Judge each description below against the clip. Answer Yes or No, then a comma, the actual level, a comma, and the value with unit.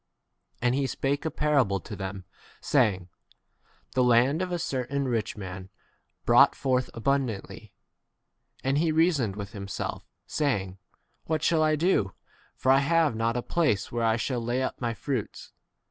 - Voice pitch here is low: Yes, low, 125 Hz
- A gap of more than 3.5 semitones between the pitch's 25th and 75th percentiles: Yes, average, 5.0 semitones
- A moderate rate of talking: Yes, average, 165 wpm